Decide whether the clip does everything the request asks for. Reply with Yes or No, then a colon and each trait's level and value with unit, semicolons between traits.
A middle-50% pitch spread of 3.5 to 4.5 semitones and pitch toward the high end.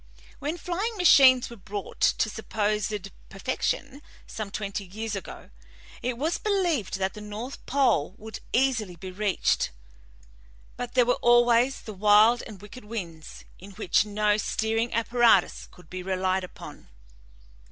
Yes: average, 4.0 semitones; high, 215 Hz